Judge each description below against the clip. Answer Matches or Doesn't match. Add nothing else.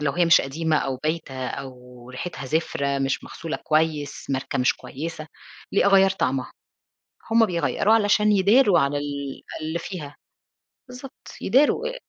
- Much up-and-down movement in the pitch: Matches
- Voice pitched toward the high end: Doesn't match